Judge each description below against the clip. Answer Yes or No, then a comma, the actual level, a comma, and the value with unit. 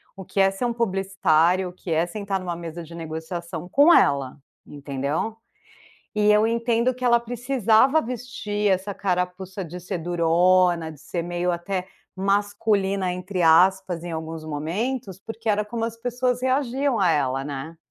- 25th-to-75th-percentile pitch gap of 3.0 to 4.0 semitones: No, average, 4.8 semitones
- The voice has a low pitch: No, high, 190 Hz